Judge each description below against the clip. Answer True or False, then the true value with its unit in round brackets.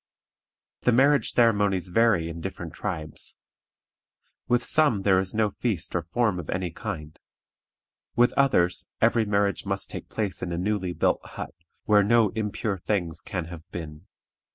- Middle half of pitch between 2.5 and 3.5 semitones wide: False (4.2 semitones)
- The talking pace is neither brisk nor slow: True (155 wpm)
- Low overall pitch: True (100 Hz)